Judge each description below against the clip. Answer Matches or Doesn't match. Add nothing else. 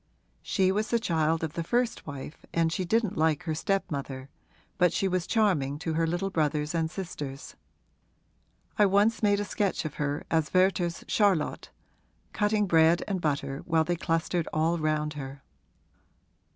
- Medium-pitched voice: Matches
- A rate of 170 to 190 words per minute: Doesn't match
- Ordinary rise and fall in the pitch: Matches